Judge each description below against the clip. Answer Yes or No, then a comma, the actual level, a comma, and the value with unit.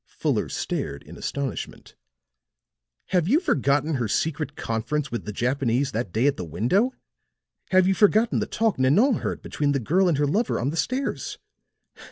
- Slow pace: No, average, 170 wpm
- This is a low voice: No, medium, 145 Hz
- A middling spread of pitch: No, wide, 7.5 semitones